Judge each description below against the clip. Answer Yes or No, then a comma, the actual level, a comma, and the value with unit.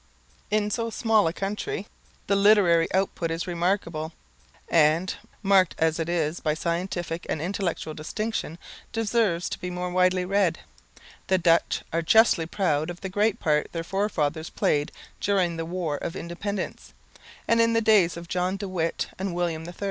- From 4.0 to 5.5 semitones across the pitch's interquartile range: No, average, 3.3 semitones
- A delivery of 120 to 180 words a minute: Yes, average, 165 wpm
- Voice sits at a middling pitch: Yes, medium, 180 Hz